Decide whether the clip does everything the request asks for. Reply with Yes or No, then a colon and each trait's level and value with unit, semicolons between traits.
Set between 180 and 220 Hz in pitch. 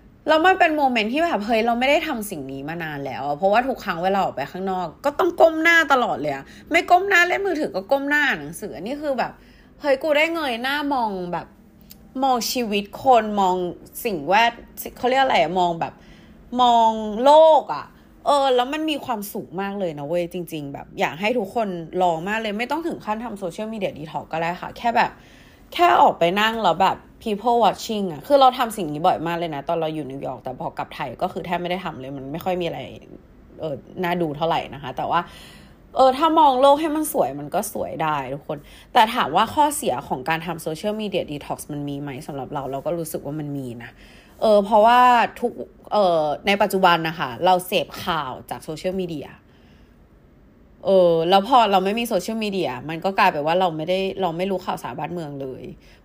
Yes: high, 190 Hz